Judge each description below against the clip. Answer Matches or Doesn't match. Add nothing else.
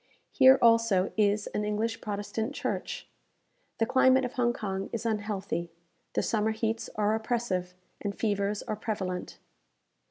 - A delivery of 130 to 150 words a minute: Matches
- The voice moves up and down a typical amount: Doesn't match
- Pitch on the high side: Matches